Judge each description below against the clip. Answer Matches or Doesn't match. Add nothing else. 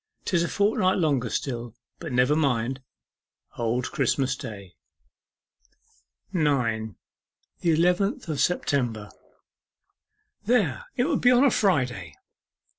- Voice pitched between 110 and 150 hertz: Matches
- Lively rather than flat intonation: Matches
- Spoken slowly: Matches